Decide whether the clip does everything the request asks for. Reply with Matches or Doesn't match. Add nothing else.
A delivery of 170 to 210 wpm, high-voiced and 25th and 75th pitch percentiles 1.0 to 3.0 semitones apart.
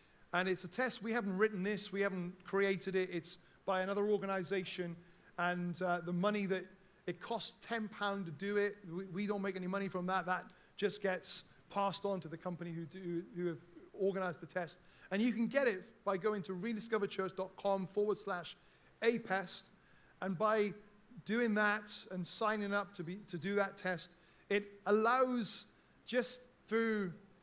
Matches